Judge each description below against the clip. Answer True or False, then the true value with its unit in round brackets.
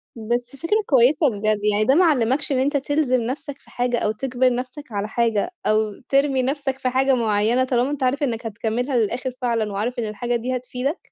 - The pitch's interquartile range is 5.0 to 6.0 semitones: False (3.1 semitones)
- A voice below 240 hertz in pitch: False (250 Hz)